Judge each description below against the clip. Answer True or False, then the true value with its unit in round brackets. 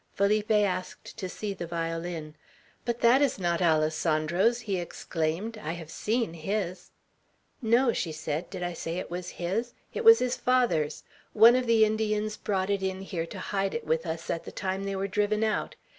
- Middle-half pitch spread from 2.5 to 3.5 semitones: False (4.4 semitones)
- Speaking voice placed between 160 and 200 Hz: True (190 Hz)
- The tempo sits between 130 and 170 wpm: False (190 wpm)